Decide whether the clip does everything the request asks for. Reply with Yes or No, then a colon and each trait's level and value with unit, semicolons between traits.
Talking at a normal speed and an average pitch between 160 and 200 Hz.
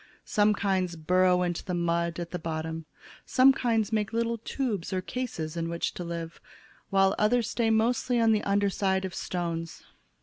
Yes: average, 175 wpm; high, 190 Hz